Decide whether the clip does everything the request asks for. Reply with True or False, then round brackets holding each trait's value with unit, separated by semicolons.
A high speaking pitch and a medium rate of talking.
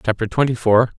False (115 Hz; 180 wpm)